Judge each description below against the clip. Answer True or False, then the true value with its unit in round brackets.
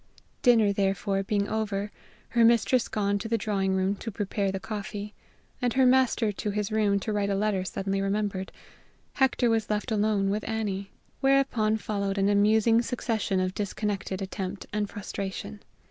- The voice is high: True (205 Hz)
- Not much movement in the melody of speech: True (2.0 semitones)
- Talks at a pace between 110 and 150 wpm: False (160 wpm)